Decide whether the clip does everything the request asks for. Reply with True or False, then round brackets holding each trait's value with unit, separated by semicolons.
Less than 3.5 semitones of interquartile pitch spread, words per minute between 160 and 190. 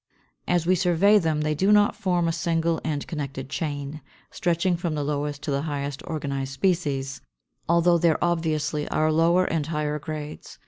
True (2.8 semitones; 170 wpm)